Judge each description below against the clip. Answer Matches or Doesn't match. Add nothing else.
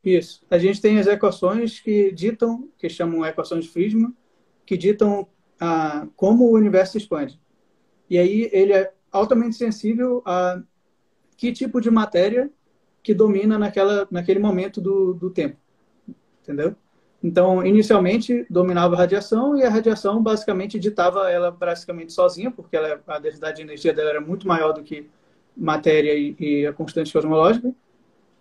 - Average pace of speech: Matches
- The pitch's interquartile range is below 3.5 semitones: Doesn't match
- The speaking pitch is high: Matches